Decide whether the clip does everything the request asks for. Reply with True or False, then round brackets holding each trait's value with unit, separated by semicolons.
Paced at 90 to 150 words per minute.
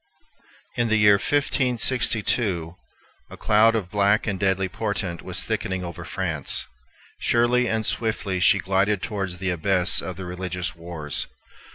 True (140 wpm)